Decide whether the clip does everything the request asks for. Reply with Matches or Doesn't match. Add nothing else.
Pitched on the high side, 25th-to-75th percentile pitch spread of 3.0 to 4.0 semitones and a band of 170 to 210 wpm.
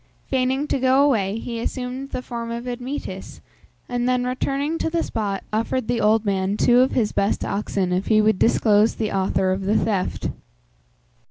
Matches